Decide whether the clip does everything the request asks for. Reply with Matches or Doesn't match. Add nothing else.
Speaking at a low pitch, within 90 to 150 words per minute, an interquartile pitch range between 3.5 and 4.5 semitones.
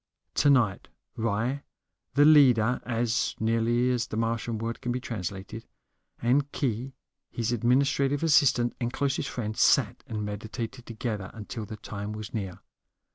Doesn't match